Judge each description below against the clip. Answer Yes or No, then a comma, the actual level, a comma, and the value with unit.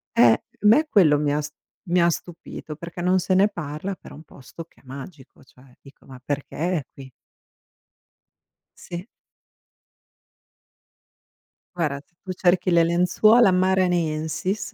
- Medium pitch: Yes, medium, 170 Hz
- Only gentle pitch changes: No, average, 4.0 semitones